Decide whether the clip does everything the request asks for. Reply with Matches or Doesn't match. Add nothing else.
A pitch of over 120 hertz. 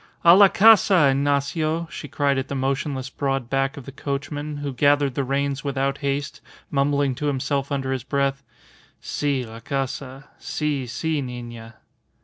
Matches